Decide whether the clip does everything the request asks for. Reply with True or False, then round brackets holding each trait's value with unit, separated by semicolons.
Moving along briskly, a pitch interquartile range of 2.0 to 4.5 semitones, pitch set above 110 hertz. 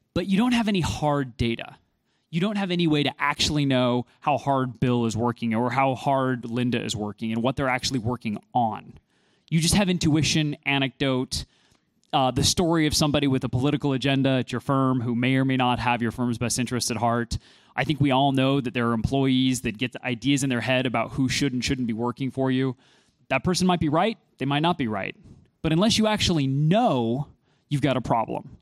True (220 wpm; 3.2 semitones; 130 Hz)